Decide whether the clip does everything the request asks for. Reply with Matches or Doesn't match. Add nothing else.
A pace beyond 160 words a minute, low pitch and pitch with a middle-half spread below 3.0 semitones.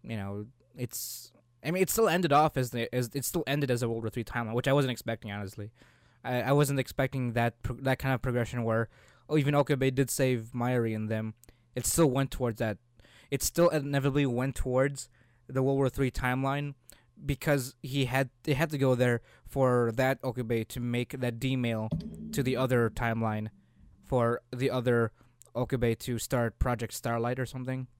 Matches